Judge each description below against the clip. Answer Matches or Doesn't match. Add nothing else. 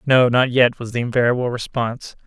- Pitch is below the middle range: Matches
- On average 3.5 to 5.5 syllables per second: Doesn't match